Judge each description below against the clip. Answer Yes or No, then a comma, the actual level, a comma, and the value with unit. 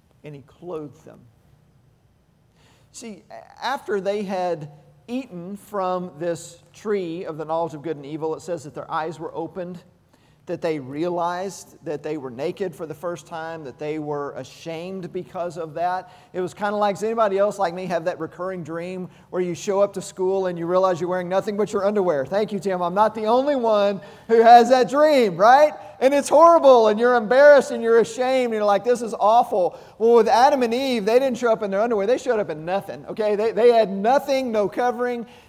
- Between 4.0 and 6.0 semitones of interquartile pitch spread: Yes, average, 5.2 semitones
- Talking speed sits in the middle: No, fast, 210 wpm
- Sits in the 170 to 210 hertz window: Yes, medium, 185 Hz